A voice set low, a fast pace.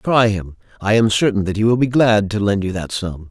Yes: low, 105 Hz; fast, 270 wpm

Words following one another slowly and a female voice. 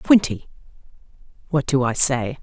Yes: slow, 125 wpm; female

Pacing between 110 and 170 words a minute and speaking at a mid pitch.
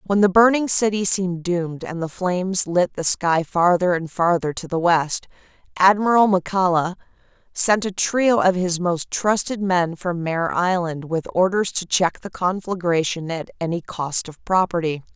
Yes: average, 165 wpm; medium, 180 Hz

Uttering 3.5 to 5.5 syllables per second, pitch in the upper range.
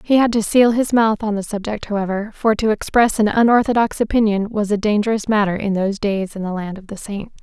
No: 5.9 syllables/s; high, 210 Hz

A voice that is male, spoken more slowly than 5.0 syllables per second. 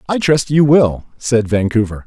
Yes: male; 4.5 syllables/s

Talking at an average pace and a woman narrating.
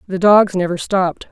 Yes: average, 180 wpm; female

